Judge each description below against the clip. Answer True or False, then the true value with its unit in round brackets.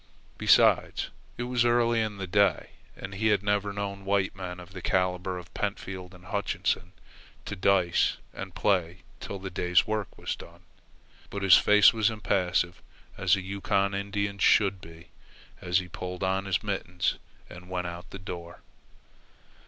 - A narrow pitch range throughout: True (2.0 semitones)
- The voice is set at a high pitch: False (95 Hz)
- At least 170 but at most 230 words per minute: False (160 wpm)